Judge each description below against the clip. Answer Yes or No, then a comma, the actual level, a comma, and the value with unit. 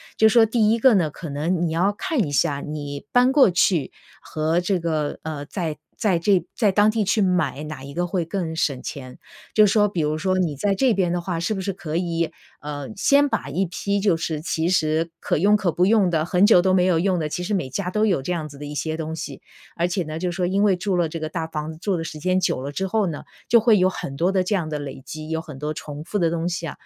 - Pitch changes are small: No, average, 3.9 semitones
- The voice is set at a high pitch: No, medium, 175 Hz